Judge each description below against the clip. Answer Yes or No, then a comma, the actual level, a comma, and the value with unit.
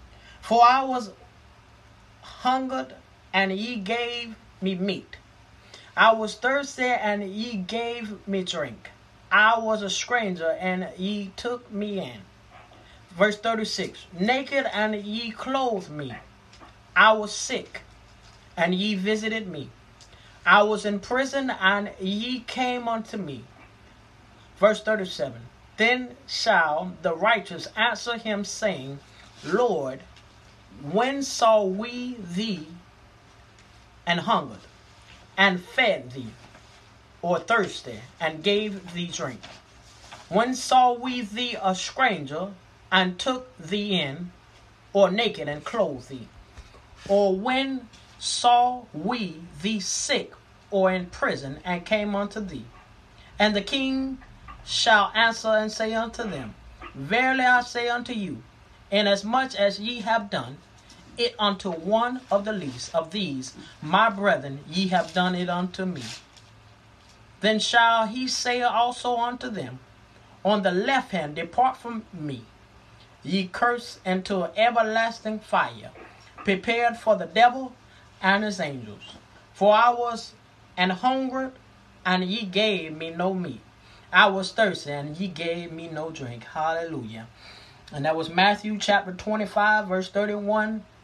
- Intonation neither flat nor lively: No, wide, 7.2 semitones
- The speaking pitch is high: Yes, high, 200 Hz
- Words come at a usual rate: No, slow, 125 wpm